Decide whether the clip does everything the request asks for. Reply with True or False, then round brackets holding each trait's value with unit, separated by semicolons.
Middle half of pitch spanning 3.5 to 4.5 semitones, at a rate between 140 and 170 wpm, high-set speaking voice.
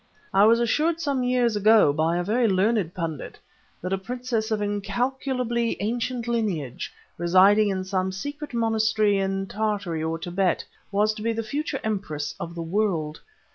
True (4.0 semitones; 160 wpm; 210 Hz)